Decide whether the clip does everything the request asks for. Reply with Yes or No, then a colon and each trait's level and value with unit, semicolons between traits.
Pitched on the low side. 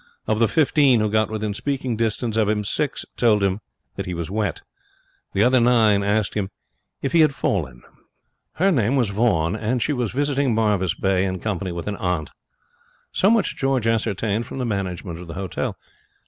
Yes: low, 110 Hz